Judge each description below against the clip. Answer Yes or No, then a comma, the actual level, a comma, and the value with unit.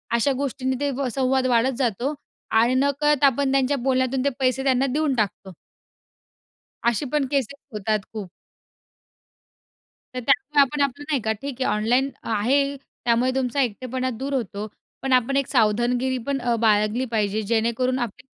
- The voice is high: Yes, very high, 255 Hz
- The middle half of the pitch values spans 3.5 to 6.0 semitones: No, average, 3.0 semitones